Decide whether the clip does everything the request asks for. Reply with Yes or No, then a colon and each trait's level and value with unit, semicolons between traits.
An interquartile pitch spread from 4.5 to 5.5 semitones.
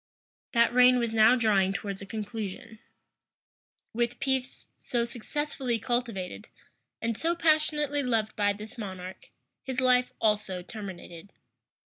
No: average, 3.6 semitones